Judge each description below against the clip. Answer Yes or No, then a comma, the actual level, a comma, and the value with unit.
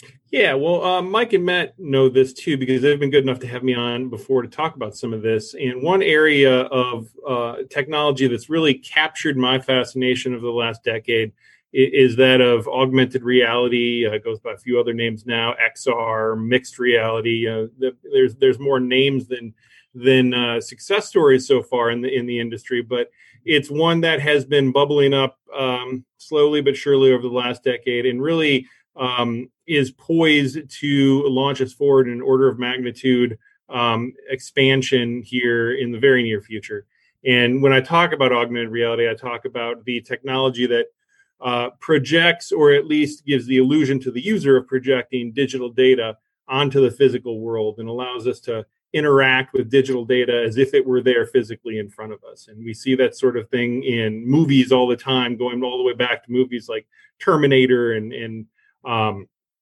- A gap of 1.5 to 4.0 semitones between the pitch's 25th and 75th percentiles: Yes, average, 2.7 semitones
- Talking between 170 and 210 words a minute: Yes, average, 185 wpm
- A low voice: Yes, low, 130 Hz